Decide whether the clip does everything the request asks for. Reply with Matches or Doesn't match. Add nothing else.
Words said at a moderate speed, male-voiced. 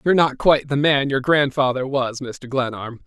Matches